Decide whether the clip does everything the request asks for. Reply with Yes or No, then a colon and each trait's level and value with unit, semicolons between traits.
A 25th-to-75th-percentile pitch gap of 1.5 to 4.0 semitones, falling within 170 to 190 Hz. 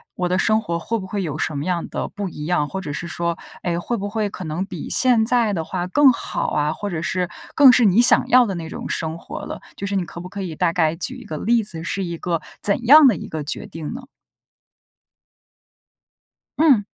No: average, 4.8 semitones; medium, 185 Hz